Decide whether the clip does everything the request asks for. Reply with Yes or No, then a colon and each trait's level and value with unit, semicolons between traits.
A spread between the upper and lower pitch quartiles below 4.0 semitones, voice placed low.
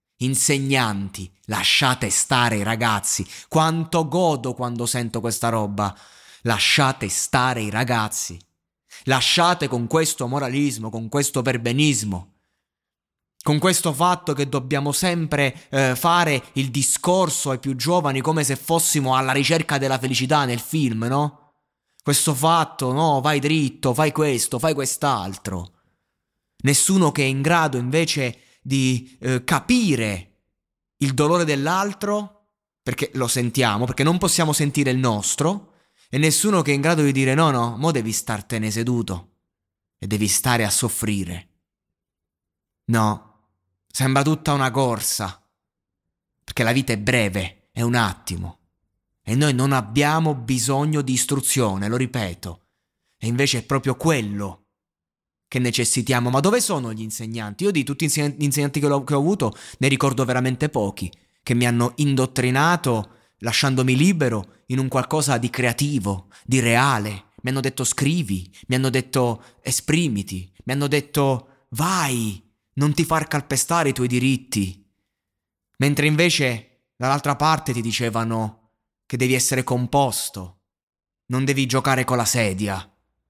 No: average, 4.7 semitones; low, 130 Hz